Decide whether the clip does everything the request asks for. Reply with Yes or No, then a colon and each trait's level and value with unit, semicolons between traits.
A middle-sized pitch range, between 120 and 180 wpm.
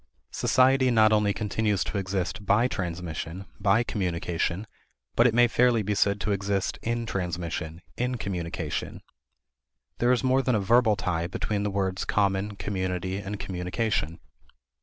Yes: average, 3.5 semitones; average, 145 wpm